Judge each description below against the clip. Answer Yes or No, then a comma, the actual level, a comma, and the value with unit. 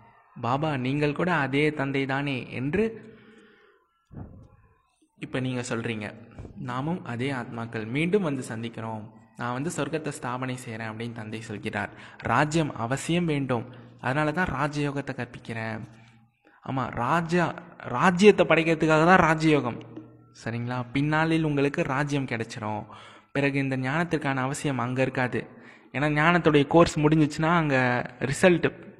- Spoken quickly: No, average, 110 wpm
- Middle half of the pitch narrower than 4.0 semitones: No, average, 5.0 semitones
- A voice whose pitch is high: No, low, 135 Hz